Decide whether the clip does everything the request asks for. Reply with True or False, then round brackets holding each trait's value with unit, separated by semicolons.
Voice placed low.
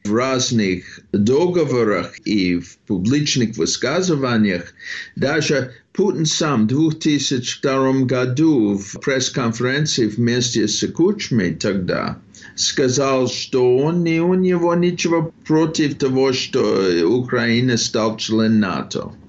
True (130 Hz)